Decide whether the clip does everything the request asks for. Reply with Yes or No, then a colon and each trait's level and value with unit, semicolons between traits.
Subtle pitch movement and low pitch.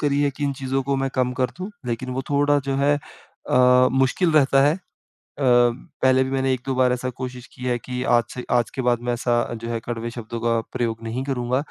Yes: narrow, 1.9 semitones; low, 130 Hz